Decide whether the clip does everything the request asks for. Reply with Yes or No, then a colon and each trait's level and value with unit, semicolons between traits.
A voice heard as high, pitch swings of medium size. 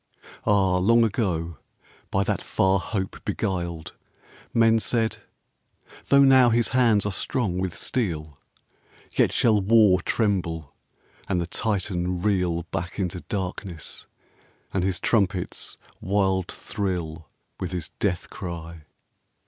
No: very low, 95 Hz; average, 3.4 semitones